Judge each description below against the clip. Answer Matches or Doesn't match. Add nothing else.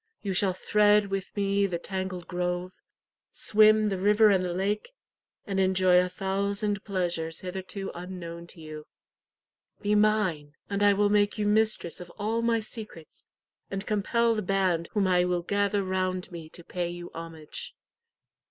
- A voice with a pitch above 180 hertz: Matches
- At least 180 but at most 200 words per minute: Doesn't match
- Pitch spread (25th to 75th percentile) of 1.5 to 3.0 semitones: Matches